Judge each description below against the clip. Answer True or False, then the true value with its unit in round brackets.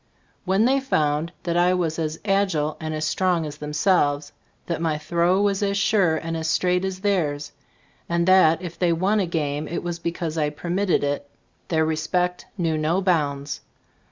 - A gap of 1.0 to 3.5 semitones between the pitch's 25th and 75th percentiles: True (3.2 semitones)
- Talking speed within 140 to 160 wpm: False (180 wpm)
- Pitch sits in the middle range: True (170 Hz)